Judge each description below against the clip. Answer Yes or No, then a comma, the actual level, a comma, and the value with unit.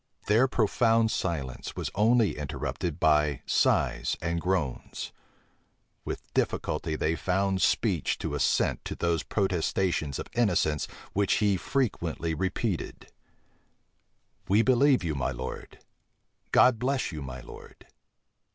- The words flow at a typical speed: No, slow, 115 wpm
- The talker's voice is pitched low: Yes, very low, 90 Hz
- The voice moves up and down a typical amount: No, wide, 6.1 semitones